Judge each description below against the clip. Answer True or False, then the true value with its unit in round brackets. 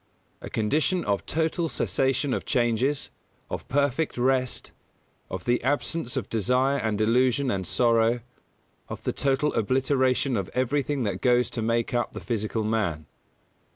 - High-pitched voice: False (125 Hz)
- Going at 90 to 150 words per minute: True (145 wpm)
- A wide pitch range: False (3.4 semitones)